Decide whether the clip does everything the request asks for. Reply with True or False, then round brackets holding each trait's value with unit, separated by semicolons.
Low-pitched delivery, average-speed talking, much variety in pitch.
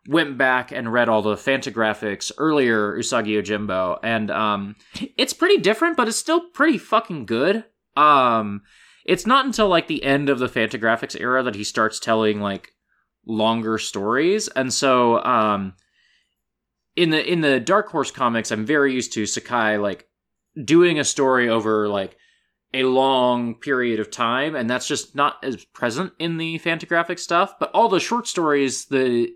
True (130 Hz; 165 wpm; 7.1 semitones)